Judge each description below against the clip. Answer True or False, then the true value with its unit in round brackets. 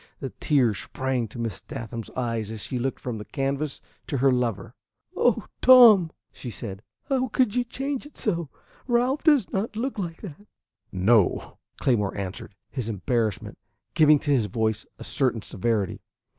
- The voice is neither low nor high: False (130 Hz)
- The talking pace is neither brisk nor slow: True (160 wpm)